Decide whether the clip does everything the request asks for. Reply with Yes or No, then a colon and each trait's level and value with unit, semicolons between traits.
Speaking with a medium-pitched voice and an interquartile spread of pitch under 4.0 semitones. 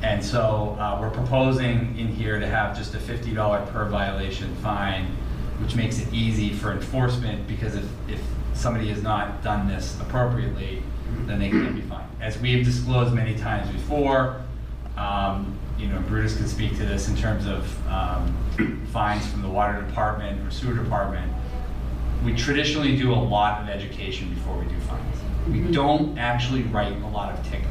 No: low, 105 Hz; average, 2.9 semitones